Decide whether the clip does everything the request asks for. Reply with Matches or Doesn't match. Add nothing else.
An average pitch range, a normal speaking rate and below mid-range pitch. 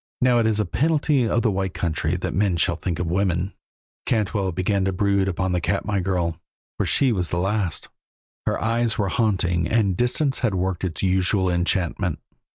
Matches